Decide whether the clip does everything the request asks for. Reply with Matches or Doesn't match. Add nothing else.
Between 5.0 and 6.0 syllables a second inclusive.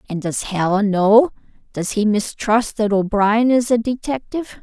Doesn't match